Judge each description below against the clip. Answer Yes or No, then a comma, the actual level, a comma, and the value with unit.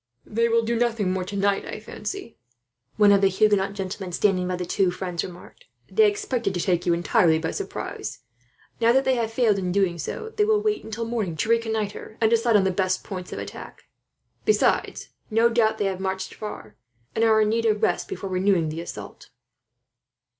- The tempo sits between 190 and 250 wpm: Yes, average, 195 wpm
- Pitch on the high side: Yes, high, 205 Hz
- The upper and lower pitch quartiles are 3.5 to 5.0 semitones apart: Yes, average, 3.8 semitones